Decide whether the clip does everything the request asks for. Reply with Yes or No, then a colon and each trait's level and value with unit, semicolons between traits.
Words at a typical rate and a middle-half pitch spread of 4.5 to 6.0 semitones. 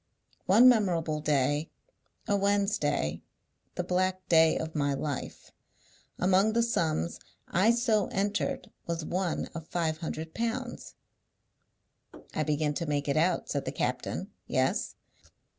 No: slow, 125 wpm; average, 4.8 semitones